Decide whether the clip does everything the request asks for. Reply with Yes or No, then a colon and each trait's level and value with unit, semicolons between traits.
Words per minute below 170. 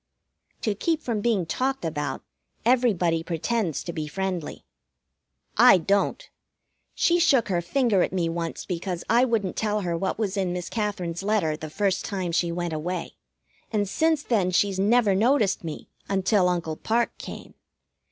Yes: average, 160 wpm